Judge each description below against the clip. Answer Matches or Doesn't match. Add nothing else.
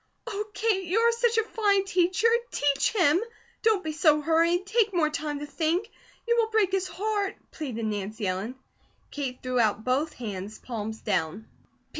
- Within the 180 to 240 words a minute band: Doesn't match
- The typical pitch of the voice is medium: Doesn't match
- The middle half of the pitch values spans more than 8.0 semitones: Matches